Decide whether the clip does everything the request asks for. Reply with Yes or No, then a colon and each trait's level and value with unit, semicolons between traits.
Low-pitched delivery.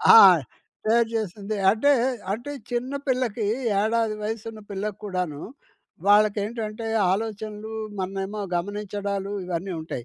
No: high, 210 Hz